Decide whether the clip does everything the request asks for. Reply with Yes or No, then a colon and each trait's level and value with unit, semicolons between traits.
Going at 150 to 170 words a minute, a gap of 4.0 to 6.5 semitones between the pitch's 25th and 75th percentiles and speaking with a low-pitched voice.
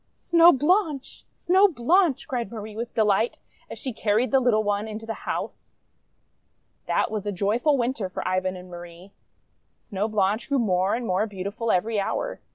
No: average, 165 wpm; average, 4.6 semitones; high, 220 Hz